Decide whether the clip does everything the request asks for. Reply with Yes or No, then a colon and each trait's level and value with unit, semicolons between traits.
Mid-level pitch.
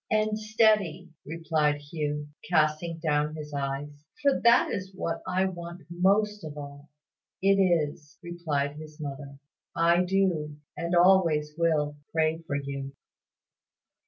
Yes: medium, 160 Hz